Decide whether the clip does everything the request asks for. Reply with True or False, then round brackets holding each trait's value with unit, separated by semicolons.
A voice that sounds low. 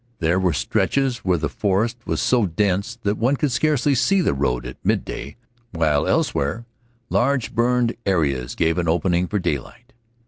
True (100 Hz)